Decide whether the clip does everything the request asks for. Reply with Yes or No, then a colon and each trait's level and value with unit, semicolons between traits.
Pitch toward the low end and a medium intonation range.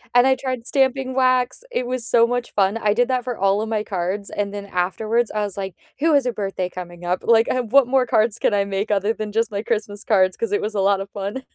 No: high, 215 Hz; average, 3.7 semitones